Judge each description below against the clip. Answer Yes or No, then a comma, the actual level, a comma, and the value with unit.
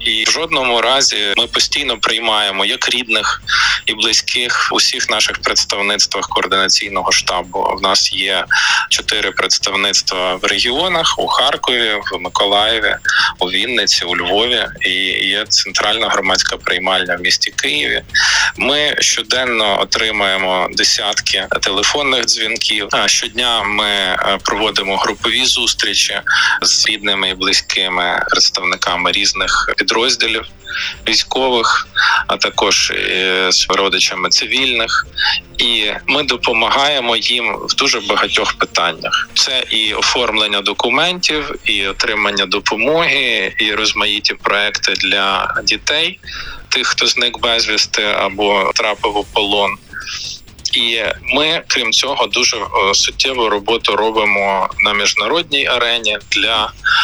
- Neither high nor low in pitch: No, low, 110 Hz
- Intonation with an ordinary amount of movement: No, wide, 7.4 semitones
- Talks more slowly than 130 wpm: Yes, average, 110 wpm